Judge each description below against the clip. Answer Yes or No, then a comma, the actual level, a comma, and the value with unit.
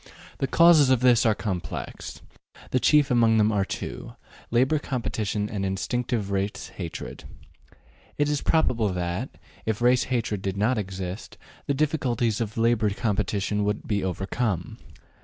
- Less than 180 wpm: Yes, average, 140 wpm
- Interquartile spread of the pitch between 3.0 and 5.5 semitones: Yes, average, 4.0 semitones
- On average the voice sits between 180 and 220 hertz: No, low, 110 Hz